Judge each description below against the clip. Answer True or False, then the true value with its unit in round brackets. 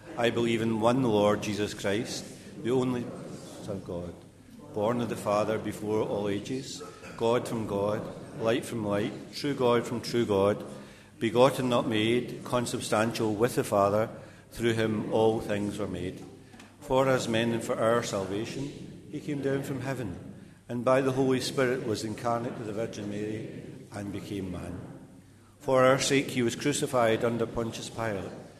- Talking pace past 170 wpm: False (165 wpm)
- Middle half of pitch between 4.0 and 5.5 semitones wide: False (3.4 semitones)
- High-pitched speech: False (115 Hz)